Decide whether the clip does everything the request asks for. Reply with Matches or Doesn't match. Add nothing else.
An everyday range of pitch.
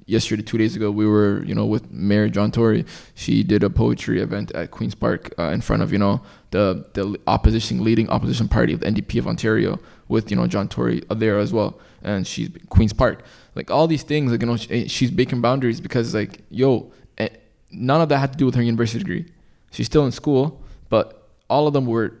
Matches